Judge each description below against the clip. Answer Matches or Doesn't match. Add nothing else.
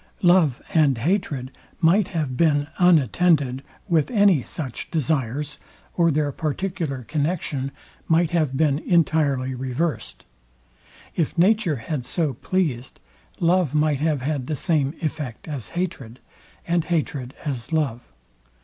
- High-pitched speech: Doesn't match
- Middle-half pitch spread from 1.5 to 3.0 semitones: Doesn't match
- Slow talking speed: Matches